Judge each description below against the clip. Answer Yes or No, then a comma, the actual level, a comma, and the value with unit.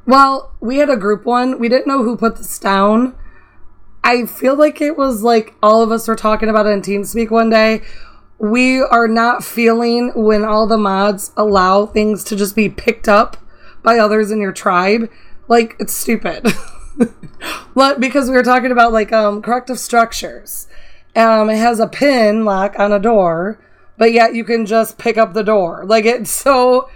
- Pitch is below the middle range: No, high, 225 Hz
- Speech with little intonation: Yes, narrow, 2.2 semitones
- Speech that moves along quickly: No, average, 185 wpm